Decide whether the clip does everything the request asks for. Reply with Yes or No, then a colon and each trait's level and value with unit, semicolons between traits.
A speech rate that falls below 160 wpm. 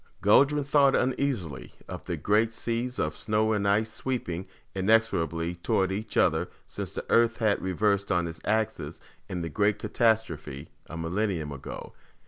Yes: average, 150 wpm